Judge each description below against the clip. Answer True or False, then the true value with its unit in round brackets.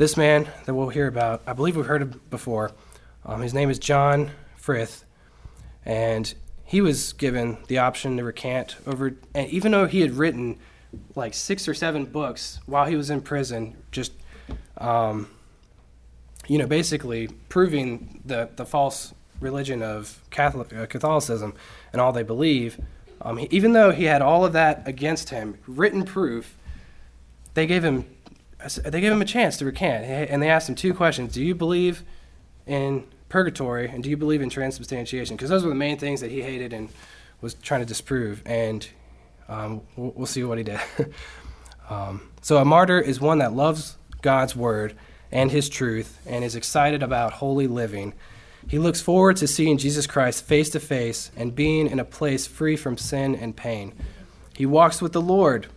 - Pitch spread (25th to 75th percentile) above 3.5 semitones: True (4.6 semitones)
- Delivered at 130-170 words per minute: False (180 wpm)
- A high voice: False (135 Hz)